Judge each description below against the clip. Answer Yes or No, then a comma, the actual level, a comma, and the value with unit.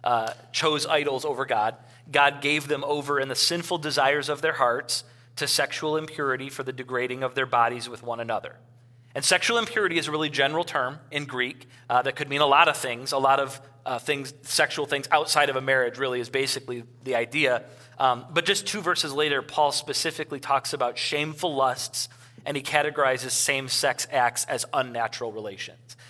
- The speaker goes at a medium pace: Yes, average, 190 wpm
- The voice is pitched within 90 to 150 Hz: Yes, medium, 140 Hz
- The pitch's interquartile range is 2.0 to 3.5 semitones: Yes, average, 3.2 semitones